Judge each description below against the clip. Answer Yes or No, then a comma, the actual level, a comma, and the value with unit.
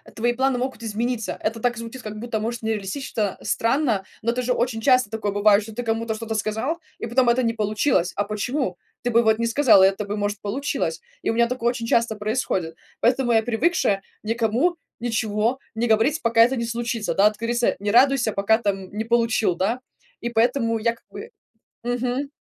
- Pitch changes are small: Yes, narrow, 2.3 semitones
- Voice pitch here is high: Yes, high, 230 Hz